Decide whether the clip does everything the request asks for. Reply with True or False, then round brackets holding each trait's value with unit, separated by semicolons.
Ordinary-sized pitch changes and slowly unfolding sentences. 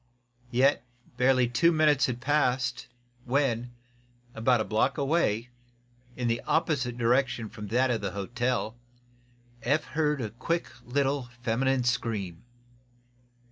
True (3.0 semitones; 120 wpm)